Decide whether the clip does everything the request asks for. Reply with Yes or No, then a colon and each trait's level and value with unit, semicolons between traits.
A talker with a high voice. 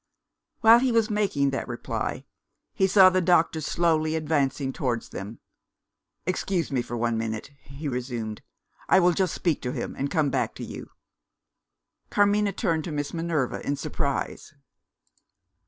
No: medium, 155 Hz